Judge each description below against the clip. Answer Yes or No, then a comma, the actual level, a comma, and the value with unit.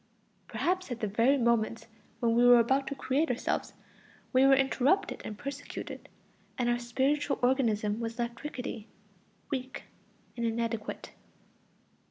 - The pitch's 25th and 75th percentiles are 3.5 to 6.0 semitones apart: No, average, 2.8 semitones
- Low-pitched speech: No, high, 245 Hz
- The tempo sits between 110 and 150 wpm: Yes, slow, 135 wpm